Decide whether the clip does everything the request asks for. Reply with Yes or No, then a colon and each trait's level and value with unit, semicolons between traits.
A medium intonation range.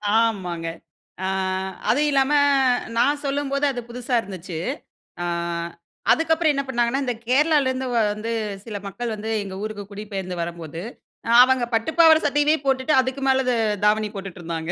No: wide, 5.7 semitones